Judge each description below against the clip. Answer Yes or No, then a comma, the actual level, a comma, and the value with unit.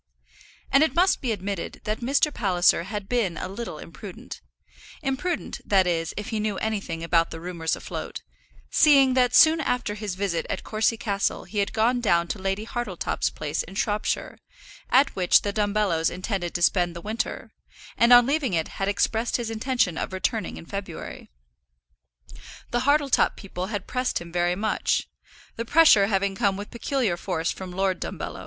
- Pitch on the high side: Yes, high, 205 Hz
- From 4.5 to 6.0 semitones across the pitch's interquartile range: Yes, average, 4.8 semitones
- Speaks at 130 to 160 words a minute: No, average, 175 wpm